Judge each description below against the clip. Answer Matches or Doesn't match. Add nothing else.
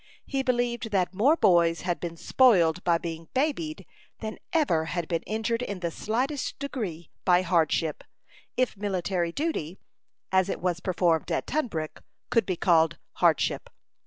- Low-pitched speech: Doesn't match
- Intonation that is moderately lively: Doesn't match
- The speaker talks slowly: Doesn't match